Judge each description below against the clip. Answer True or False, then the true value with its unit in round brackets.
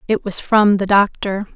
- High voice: True (200 Hz)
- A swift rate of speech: False (195 wpm)